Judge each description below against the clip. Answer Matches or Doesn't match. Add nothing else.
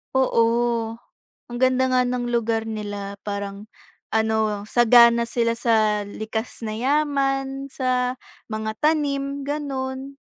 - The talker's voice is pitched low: Doesn't match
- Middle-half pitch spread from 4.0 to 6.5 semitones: Doesn't match